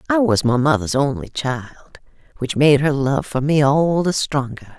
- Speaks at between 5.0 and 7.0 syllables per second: No, 4.8 syllables/s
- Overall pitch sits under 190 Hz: Yes, medium, 140 Hz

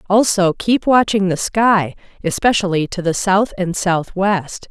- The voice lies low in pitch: No, high, 190 Hz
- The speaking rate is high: No, average, 140 wpm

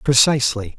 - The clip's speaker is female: No, male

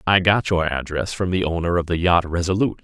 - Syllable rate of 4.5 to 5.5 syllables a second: No, 6.0 syllables/s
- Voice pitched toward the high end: No, very low, 90 Hz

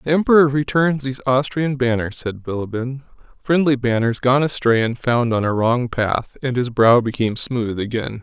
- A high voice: No, low, 125 Hz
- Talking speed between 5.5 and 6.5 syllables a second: No, 5.0 syllables/s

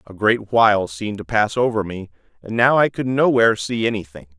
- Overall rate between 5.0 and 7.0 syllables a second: Yes, 5.7 syllables/s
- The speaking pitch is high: No, low, 110 Hz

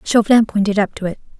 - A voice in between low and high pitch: No, high, 205 Hz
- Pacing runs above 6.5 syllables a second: Yes, 7.1 syllables/s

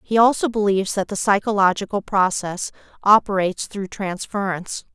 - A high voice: Yes, high, 200 Hz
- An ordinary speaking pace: No, slow, 120 wpm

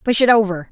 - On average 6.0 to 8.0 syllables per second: Yes, 6.6 syllables/s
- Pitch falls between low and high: No, high, 205 Hz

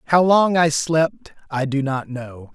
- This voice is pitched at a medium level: Yes, medium, 150 Hz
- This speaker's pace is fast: No, average, 190 wpm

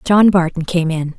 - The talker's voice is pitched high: No, medium, 175 Hz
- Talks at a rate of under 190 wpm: No, average, 200 wpm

